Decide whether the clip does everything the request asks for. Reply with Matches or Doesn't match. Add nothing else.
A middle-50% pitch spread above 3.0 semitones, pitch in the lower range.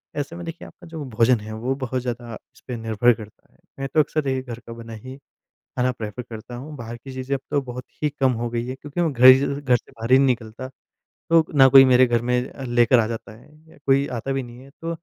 Doesn't match